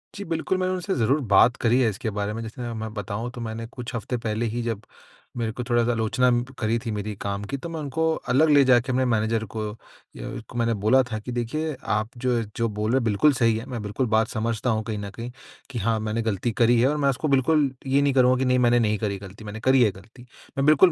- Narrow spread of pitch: No, average, 3.0 semitones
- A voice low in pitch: Yes, low, 120 Hz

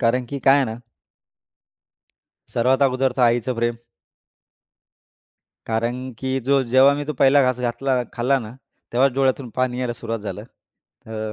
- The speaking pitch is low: Yes, low, 125 Hz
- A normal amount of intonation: No, narrow, 2.2 semitones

